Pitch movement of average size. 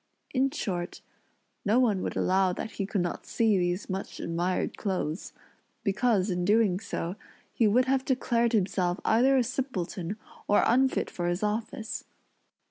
Yes: average, 4.5 semitones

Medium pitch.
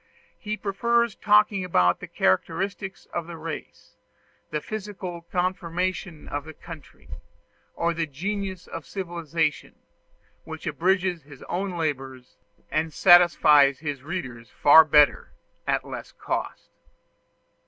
Yes: medium, 170 Hz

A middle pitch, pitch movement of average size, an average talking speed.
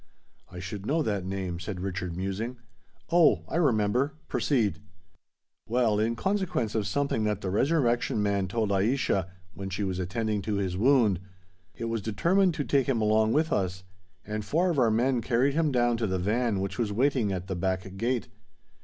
No: low, 110 Hz; average, 4.8 semitones; average, 180 wpm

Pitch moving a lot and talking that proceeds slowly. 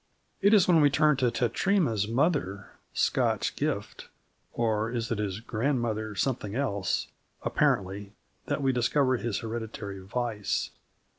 No: average, 4.7 semitones; slow, 130 wpm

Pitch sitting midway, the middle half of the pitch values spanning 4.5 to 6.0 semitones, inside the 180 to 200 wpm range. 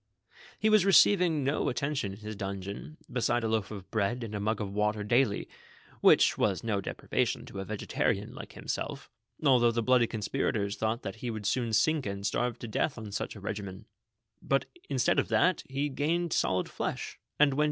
No: low, 110 Hz; average, 4.8 semitones; average, 195 wpm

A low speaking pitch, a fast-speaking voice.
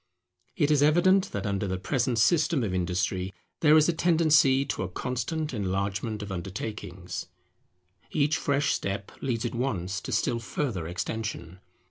No: low, 115 Hz; average, 150 wpm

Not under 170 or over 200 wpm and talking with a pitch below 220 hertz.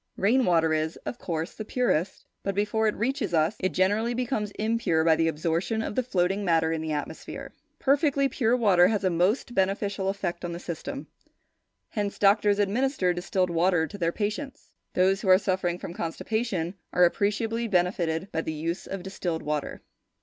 Yes: average, 180 wpm; high, 190 Hz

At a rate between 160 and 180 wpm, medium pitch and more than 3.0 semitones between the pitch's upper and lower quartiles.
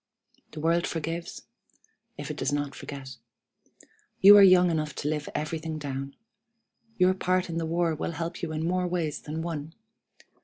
No: average, 165 wpm; medium, 165 Hz; narrow, 2.4 semitones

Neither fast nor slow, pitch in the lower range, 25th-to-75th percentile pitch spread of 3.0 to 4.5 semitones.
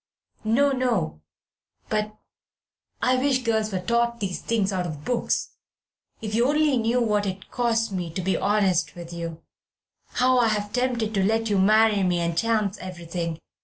No: average, 170 wpm; high, 215 Hz; average, 4.1 semitones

